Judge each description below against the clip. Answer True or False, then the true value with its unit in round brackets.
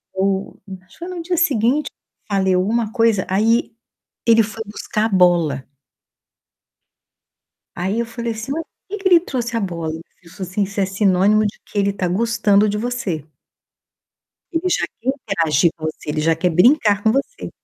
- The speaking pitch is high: True (210 Hz)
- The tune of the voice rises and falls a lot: False (4.2 semitones)